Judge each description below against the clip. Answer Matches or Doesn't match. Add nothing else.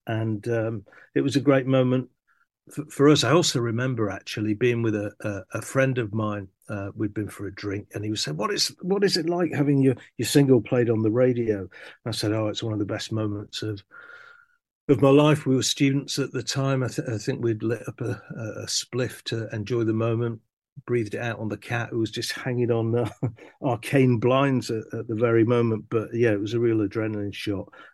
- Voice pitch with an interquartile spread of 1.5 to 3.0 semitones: Doesn't match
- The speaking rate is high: Matches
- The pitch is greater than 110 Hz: Matches